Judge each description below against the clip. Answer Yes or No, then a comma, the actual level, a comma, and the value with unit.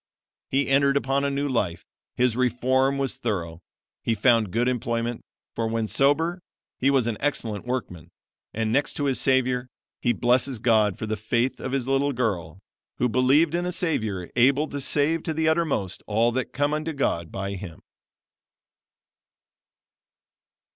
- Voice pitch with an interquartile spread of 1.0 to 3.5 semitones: No, average, 4.0 semitones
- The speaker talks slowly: No, average, 160 wpm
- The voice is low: Yes, low, 125 Hz